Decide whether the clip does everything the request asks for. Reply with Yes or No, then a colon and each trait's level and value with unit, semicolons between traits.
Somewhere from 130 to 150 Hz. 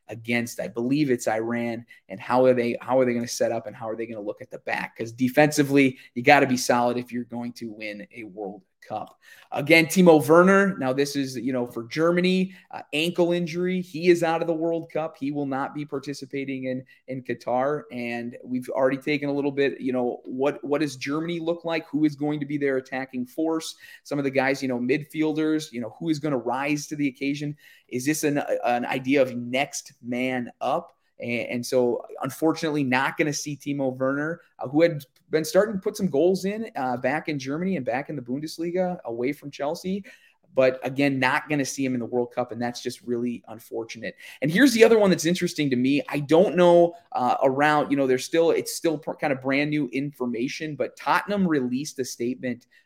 Yes: medium, 140 Hz